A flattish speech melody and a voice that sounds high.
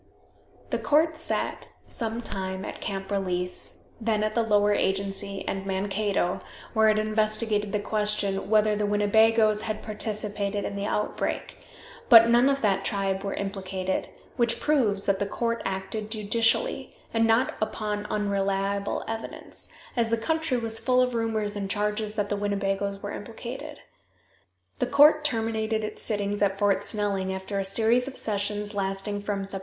Yes: narrow, 2.2 semitones; high, 210 Hz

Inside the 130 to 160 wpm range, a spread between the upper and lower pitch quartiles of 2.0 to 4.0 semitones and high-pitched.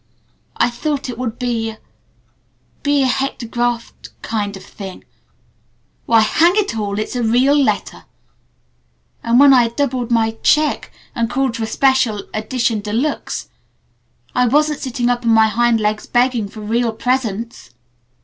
Yes: average, 155 wpm; average, 2.8 semitones; high, 240 Hz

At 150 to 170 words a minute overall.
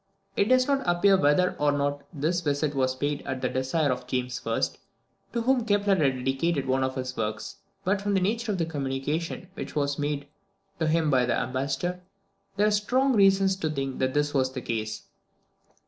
No: average, 195 wpm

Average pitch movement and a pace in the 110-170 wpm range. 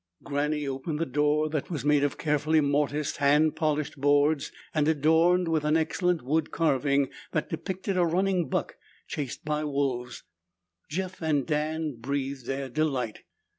No: narrow, 2.1 semitones; average, 150 wpm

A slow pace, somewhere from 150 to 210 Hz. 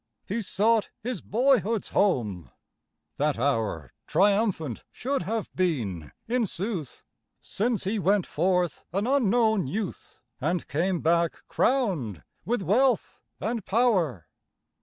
Yes: slow, 115 wpm; high, 190 Hz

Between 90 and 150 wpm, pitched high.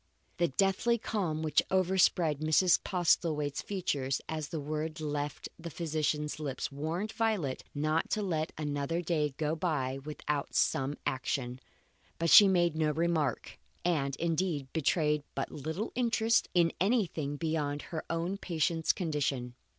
No: slow, 135 wpm; medium, 155 Hz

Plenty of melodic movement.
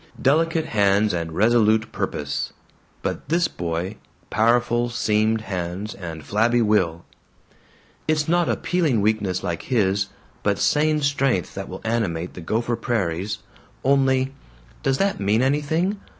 Yes: wide, 5.7 semitones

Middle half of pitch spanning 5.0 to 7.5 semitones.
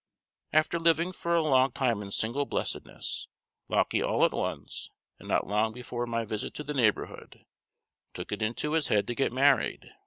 Yes: wide, 5.4 semitones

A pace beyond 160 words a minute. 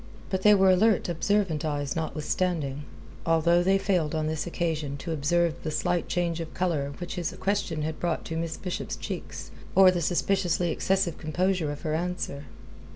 Yes: average, 170 wpm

